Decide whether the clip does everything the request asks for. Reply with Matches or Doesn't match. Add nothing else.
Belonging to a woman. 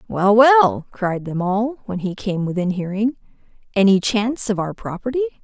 Matches